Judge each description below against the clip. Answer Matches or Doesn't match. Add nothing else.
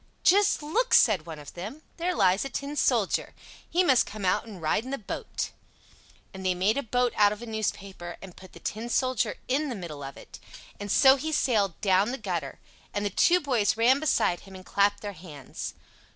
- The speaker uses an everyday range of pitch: Doesn't match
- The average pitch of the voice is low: Doesn't match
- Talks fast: Matches